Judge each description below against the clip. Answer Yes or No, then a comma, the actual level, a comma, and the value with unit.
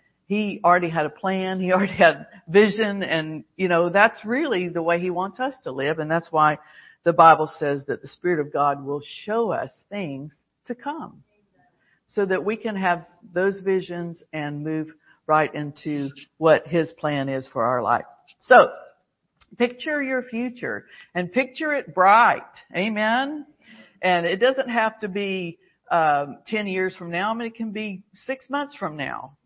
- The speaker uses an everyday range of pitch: No, wide, 5.8 semitones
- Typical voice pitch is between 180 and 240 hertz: Yes, medium, 185 Hz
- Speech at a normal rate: Yes, average, 175 wpm